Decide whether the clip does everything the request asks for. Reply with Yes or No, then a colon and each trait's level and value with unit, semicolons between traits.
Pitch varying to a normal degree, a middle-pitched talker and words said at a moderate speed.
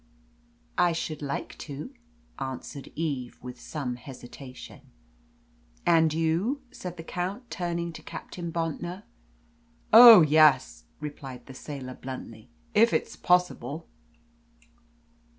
No: average, 4.5 semitones; medium, 155 Hz; slow, 105 wpm